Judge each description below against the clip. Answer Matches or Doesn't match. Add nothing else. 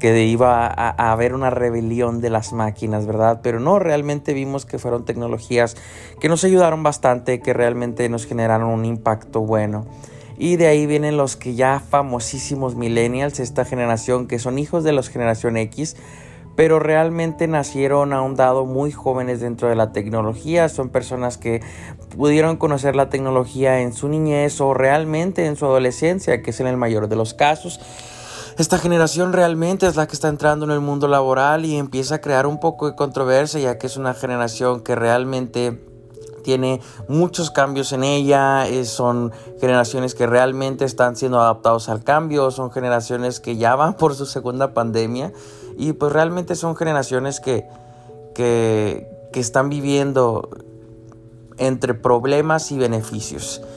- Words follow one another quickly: Doesn't match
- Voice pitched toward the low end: Matches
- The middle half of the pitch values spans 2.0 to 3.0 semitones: Doesn't match